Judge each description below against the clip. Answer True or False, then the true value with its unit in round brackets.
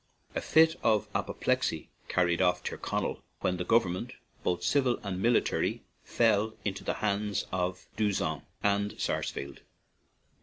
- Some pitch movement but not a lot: True (3.4 semitones)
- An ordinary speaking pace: False (130 wpm)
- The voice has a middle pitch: False (100 Hz)